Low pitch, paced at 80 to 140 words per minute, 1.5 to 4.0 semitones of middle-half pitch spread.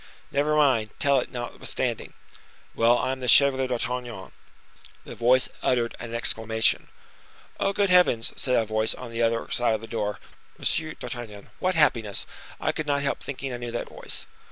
No: low, 120 Hz; average, 175 wpm; average, 3.4 semitones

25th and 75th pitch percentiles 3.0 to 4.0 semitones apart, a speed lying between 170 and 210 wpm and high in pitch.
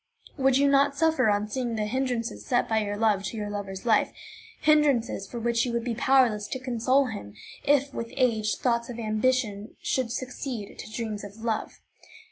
Yes: average, 3.3 semitones; average, 185 wpm; high, 235 Hz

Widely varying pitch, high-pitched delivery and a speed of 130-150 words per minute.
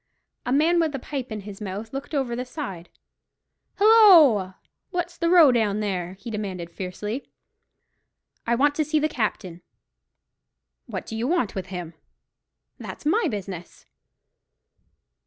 Yes: wide, 7.7 semitones; high, 235 Hz; average, 140 wpm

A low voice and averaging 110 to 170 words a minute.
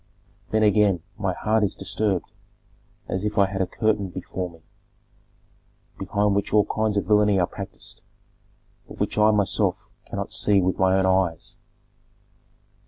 Yes: low, 100 Hz; average, 150 wpm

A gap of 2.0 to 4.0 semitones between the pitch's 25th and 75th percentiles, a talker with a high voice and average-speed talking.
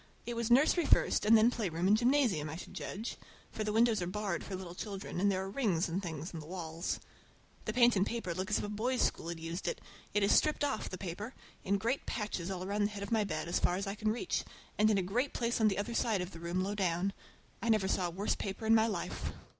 No: average, 3.6 semitones; high, 200 Hz; fast, 265 wpm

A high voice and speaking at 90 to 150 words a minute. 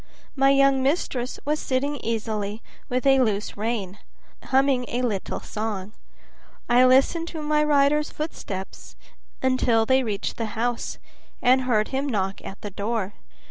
Yes: very high, 250 Hz; average, 140 wpm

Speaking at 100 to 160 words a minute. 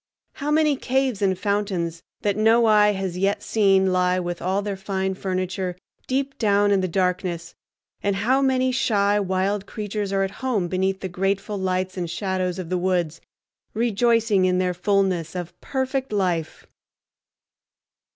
Yes: average, 155 wpm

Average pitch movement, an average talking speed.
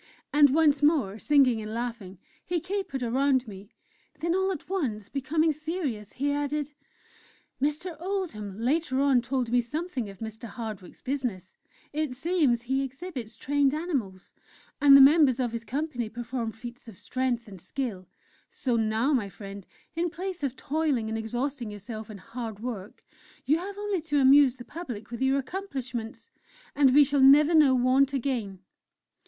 Yes: average, 4.7 semitones; average, 160 wpm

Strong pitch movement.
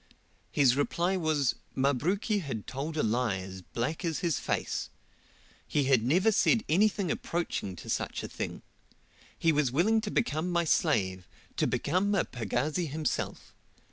Yes: wide, 6.1 semitones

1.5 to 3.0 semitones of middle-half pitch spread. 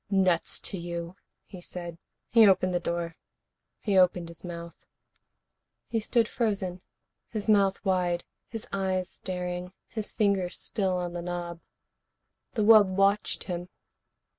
Yes: narrow, 2.4 semitones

